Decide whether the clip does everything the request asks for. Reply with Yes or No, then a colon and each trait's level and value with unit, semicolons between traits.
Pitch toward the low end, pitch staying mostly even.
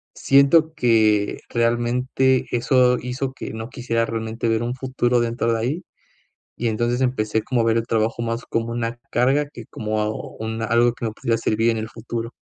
Yes: low, 115 Hz; narrow, 1.7 semitones